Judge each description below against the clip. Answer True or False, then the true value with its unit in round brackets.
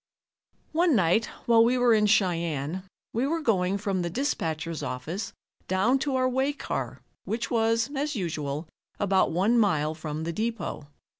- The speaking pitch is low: False (205 Hz)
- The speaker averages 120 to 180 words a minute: True (155 wpm)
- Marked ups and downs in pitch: True (6.2 semitones)